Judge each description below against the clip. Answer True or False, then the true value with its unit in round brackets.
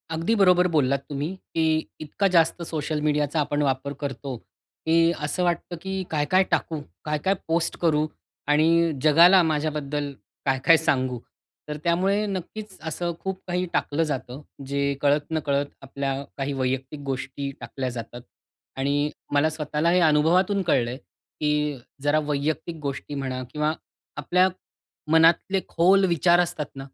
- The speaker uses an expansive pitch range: False (3.4 semitones)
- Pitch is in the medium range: True (150 Hz)